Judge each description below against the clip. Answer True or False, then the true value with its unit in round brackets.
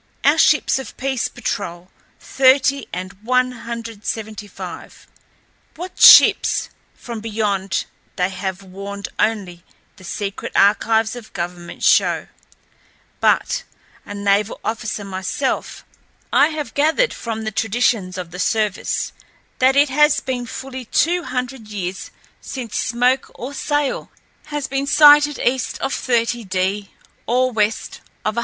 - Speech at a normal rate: False (130 wpm)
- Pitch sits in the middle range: False (225 Hz)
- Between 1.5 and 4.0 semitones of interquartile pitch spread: False (4.7 semitones)